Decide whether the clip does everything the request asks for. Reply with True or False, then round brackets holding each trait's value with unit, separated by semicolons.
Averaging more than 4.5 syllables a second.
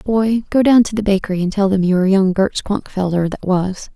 True (5.6 syllables/s)